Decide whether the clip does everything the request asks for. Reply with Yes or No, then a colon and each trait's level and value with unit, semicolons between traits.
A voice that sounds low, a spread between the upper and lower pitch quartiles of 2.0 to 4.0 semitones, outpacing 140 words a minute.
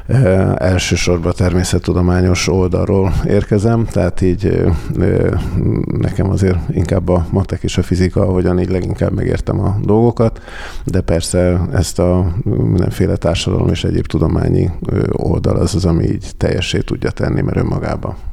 No: very low, 95 Hz; average, 2.7 semitones; average, 130 wpm